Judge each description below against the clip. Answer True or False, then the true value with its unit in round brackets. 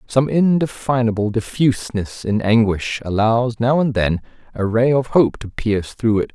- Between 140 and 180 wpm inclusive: True (160 wpm)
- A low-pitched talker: True (115 Hz)